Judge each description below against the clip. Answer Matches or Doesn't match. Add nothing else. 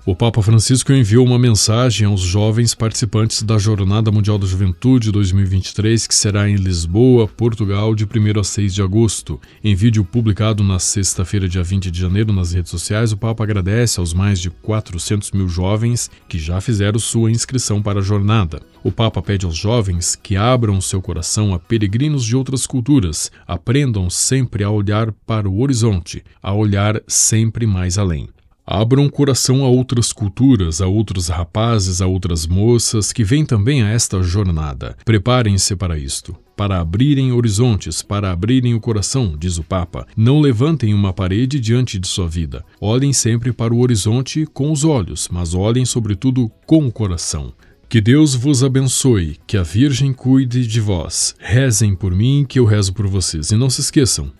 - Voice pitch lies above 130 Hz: Doesn't match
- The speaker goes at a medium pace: Matches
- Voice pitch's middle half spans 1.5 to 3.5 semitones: Doesn't match